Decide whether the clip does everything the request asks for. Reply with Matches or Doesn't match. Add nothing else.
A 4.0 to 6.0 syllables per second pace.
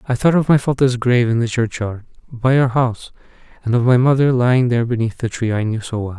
Doesn't match